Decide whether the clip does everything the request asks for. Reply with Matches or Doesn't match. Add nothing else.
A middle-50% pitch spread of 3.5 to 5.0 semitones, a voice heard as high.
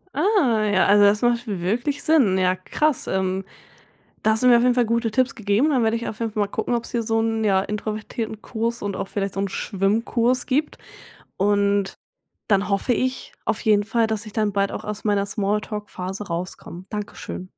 Doesn't match